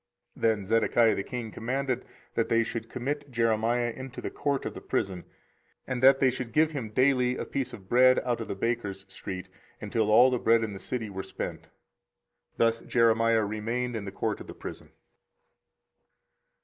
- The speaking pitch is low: Yes, low, 115 Hz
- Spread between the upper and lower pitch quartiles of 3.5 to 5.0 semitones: No, narrow, 2.5 semitones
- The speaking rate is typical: Yes, average, 185 wpm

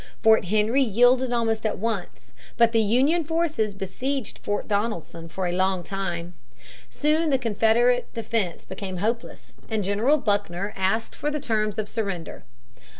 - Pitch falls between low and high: No, high, 220 Hz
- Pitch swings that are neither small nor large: Yes, average, 4.0 semitones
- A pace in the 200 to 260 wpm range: No, average, 150 wpm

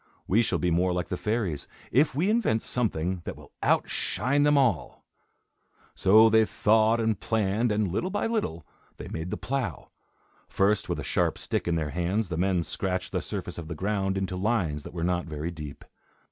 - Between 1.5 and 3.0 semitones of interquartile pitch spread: No, average, 4.6 semitones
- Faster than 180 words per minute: Yes, average, 190 wpm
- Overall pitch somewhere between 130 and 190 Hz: No, very low, 95 Hz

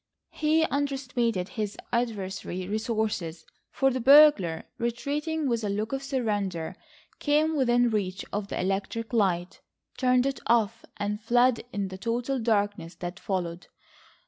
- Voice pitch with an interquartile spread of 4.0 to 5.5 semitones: Yes, average, 4.8 semitones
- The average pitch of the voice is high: Yes, high, 225 Hz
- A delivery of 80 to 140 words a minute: Yes, slow, 135 wpm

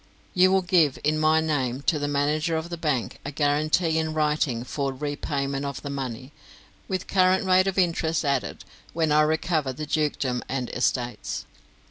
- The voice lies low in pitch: No, medium, 150 Hz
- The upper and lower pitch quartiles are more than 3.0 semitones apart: No, average, 2.7 semitones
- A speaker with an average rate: Yes, average, 170 wpm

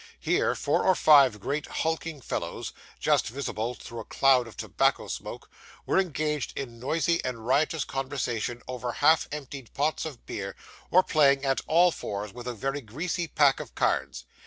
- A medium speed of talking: Yes, average, 165 wpm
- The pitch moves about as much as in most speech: Yes, average, 4.2 semitones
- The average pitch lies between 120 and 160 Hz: Yes, low, 135 Hz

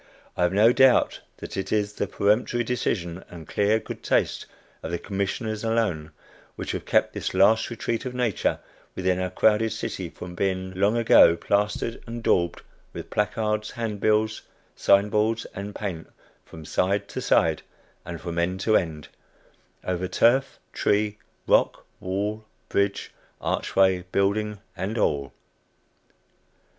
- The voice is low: Yes, low, 100 Hz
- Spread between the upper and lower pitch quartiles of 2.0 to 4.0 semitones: Yes, average, 2.9 semitones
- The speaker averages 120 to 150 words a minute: Yes, average, 140 wpm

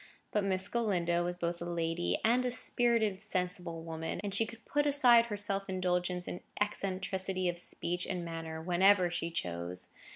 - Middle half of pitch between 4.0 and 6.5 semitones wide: No, average, 3.1 semitones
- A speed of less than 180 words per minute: Yes, average, 170 wpm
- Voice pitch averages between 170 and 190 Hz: Yes, medium, 185 Hz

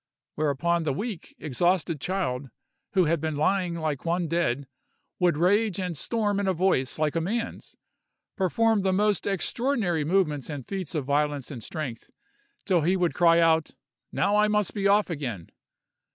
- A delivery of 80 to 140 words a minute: No, average, 165 wpm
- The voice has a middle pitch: Yes, medium, 170 Hz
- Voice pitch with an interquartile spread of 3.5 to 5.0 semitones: Yes, average, 4.5 semitones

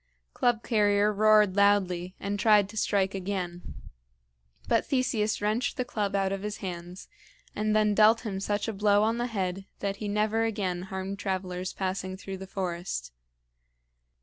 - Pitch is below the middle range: No, high, 200 Hz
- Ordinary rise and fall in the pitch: No, narrow, 2.1 semitones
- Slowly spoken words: No, average, 160 wpm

